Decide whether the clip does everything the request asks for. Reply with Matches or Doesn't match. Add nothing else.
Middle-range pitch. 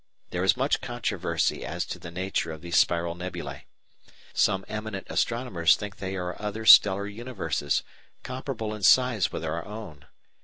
Doesn't match